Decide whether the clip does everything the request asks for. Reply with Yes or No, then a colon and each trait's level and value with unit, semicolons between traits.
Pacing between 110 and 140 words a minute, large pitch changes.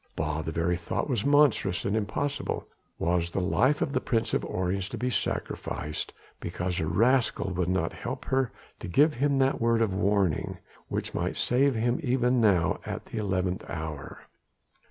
No: average, 175 wpm; wide, 6.0 semitones